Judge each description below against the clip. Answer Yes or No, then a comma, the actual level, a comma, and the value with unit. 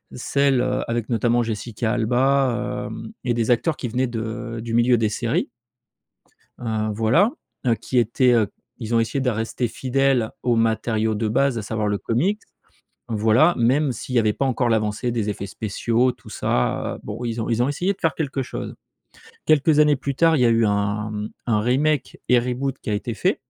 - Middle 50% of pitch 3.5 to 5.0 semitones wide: No, average, 2.9 semitones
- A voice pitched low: Yes, low, 120 Hz